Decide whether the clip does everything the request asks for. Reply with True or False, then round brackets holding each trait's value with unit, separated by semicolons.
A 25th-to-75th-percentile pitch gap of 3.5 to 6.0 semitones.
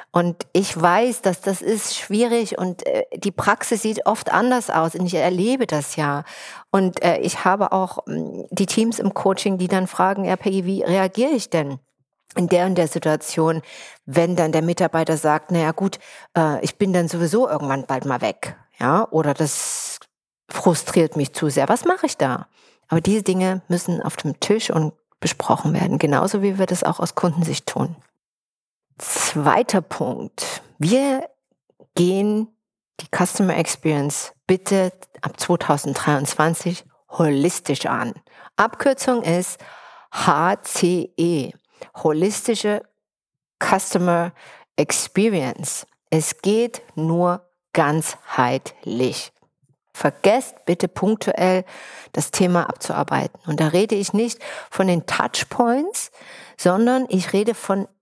True (3.9 semitones)